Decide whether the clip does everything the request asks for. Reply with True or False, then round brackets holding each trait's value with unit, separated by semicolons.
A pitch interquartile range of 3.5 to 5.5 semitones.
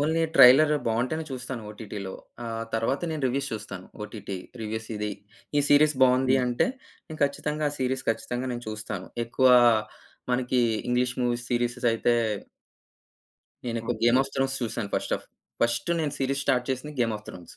False (2.9 semitones)